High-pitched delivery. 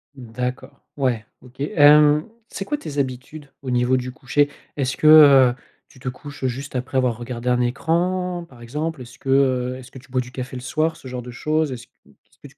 No: low, 130 Hz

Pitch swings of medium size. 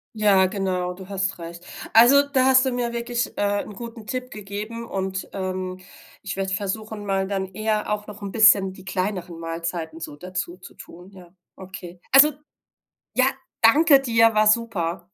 Yes: average, 3.5 semitones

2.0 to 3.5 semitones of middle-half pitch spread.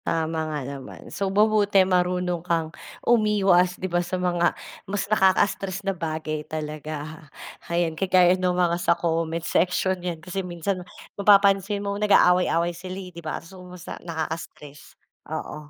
Yes: average, 2.8 semitones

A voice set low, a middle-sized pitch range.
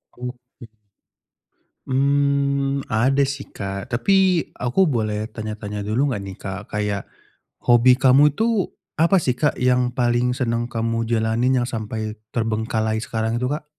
Yes: low, 125 Hz; average, 3.8 semitones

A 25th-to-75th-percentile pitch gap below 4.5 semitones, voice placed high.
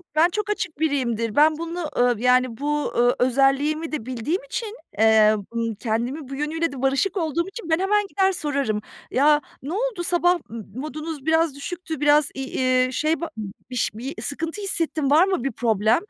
No: average, 4.8 semitones; very high, 295 Hz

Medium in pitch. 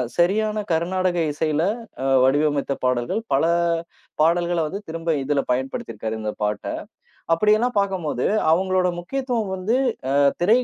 Yes: medium, 170 Hz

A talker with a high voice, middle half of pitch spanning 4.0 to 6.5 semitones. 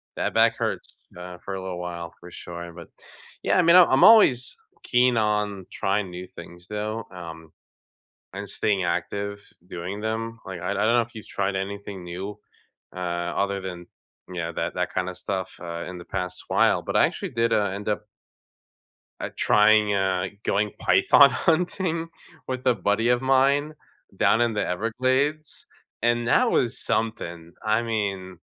No: low, 100 Hz; average, 4.5 semitones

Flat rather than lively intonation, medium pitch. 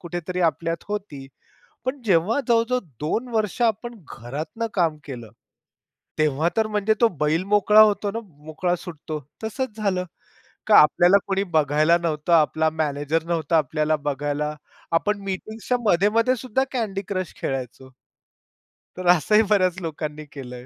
No: wide, 5.6 semitones; medium, 175 Hz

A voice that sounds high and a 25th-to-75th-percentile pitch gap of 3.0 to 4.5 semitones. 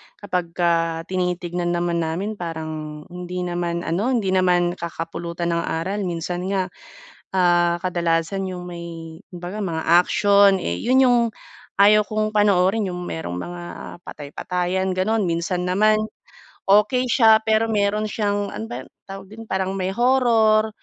No: medium, 180 Hz; average, 3.3 semitones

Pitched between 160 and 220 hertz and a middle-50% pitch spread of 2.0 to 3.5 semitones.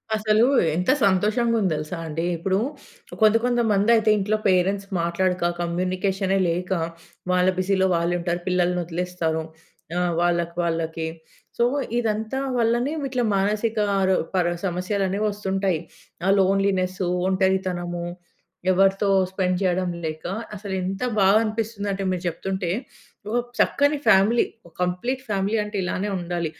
Yes: high, 190 Hz; average, 2.8 semitones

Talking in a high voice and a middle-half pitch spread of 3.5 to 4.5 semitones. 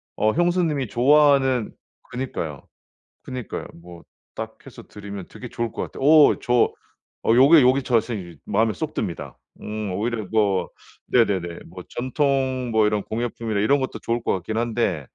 No: low, 115 Hz; average, 3.9 semitones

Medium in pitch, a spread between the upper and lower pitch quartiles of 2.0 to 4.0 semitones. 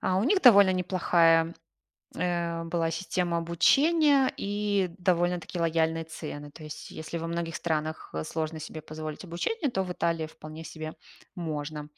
Yes: medium, 170 Hz; narrow, 2.5 semitones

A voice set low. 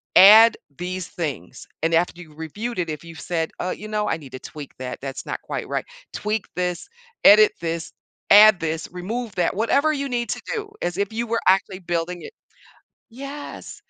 No: medium, 180 Hz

